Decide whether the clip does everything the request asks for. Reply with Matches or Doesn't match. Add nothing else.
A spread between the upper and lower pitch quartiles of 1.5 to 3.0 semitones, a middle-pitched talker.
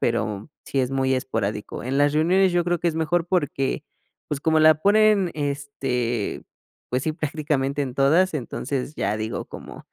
Doesn't match